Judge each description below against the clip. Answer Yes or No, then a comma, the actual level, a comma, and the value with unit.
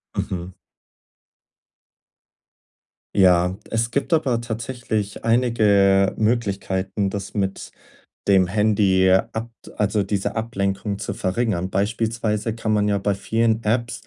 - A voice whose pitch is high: No, low, 105 Hz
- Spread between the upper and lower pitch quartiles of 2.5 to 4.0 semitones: Yes, average, 2.8 semitones